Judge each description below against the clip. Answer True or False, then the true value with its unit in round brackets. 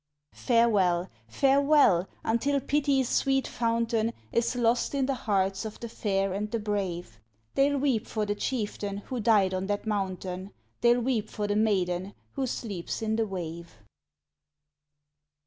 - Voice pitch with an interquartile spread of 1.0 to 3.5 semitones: False (3.9 semitones)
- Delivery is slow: False (145 wpm)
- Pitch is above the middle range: True (215 Hz)